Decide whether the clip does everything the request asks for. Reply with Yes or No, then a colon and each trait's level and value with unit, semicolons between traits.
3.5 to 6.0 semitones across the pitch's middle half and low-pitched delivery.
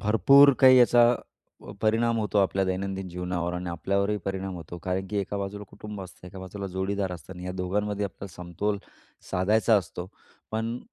No: narrow, 2.5 semitones; low, 100 Hz